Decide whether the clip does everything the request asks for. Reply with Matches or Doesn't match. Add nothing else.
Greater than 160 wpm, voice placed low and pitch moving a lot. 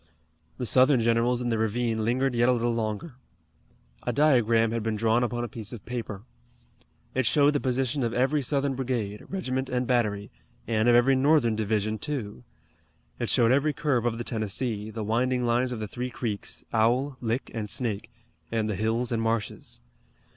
Doesn't match